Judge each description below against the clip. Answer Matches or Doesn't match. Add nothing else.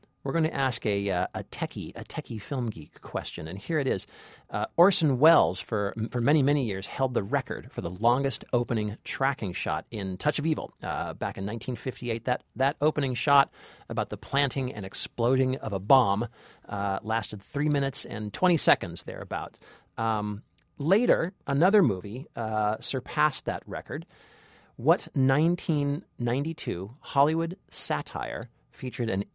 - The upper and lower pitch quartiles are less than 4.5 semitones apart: Doesn't match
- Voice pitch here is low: Matches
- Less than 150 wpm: Doesn't match